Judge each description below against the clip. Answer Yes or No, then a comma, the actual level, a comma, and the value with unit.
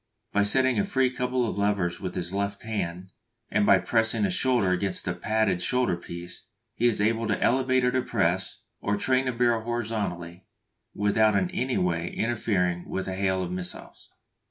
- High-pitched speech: No, low, 105 Hz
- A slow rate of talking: No, average, 175 wpm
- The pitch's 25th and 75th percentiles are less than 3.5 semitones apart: No, average, 4.7 semitones